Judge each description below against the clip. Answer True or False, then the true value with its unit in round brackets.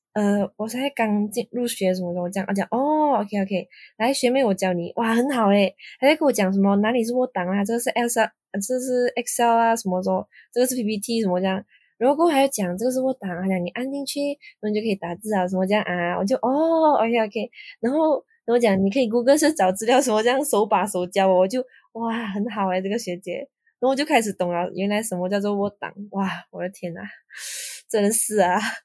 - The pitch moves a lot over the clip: False (4.7 semitones)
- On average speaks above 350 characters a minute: True (370 characters per minute)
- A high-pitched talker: True (215 Hz)